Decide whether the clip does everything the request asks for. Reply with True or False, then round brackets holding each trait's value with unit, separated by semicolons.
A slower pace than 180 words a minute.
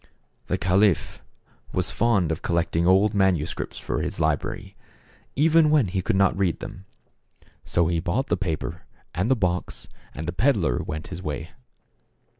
True (160 wpm)